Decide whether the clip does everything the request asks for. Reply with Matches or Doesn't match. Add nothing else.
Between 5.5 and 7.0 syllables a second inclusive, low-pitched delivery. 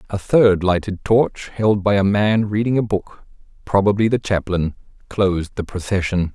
Doesn't match